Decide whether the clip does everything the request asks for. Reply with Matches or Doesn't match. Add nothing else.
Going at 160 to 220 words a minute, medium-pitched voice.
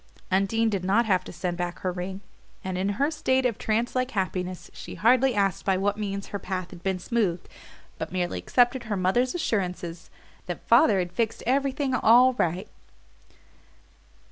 Doesn't match